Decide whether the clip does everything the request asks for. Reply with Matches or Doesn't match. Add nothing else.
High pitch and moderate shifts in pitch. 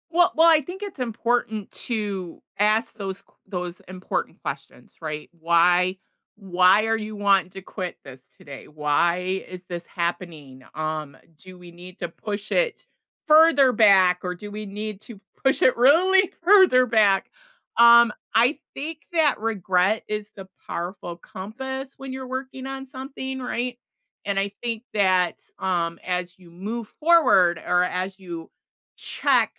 Doesn't match